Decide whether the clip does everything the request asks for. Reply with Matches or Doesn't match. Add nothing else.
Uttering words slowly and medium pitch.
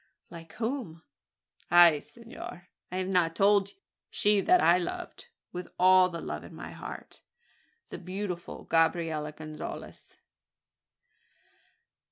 Matches